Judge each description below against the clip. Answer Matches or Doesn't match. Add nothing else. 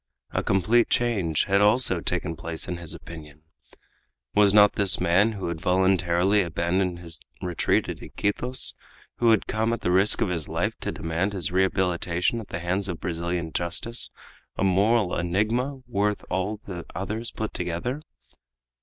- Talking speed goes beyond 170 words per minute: Doesn't match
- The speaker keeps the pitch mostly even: Doesn't match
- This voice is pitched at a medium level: Doesn't match